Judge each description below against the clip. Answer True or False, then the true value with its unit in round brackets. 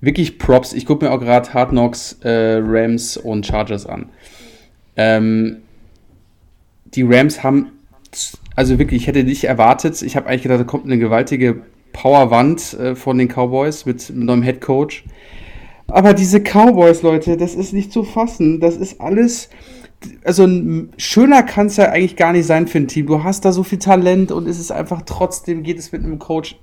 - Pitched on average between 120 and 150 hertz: True (140 Hz)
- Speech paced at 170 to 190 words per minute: True (185 wpm)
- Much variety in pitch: True (6.2 semitones)